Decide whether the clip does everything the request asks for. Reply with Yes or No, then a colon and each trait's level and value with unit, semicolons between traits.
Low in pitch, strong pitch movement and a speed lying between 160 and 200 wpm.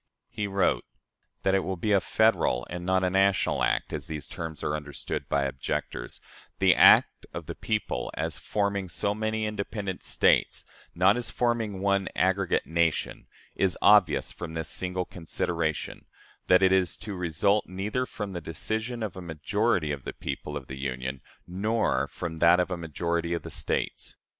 No: very low, 90 Hz; average, 3.8 semitones; average, 170 wpm